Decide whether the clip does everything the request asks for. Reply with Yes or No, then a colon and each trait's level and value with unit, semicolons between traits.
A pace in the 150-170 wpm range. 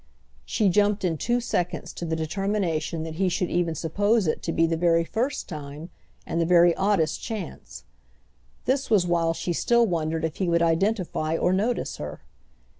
No: average, 180 wpm